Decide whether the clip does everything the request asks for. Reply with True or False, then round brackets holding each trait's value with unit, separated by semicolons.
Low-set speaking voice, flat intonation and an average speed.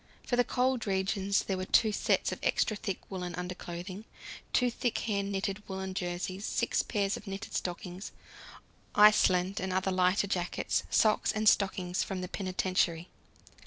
False (190 Hz; 2.3 semitones; 155 wpm)